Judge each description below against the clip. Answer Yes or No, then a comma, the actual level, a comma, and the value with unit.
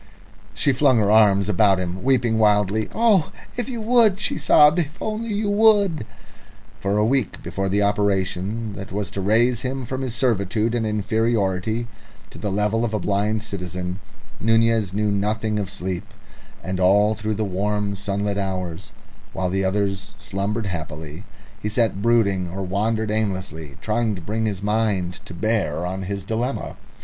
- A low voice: Yes, low, 105 Hz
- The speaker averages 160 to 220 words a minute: Yes, average, 165 wpm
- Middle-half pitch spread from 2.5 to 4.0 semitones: Yes, average, 2.8 semitones